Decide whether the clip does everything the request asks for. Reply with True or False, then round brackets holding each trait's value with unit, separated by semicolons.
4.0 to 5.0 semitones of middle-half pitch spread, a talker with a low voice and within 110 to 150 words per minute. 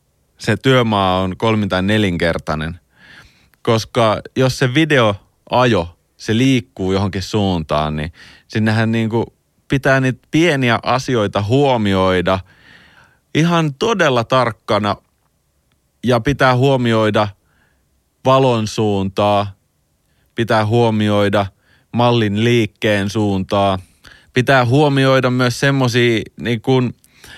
False (4.6 semitones; 110 Hz; 95 wpm)